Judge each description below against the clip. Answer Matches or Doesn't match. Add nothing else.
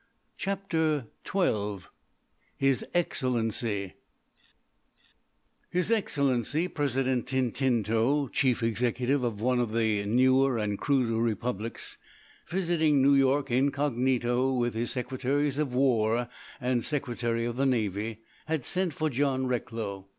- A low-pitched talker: Matches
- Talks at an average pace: Doesn't match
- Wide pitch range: Doesn't match